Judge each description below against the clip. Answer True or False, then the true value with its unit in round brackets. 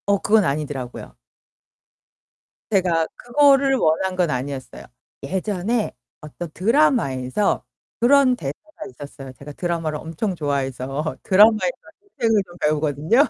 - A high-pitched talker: False (170 Hz)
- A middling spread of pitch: False (7.4 semitones)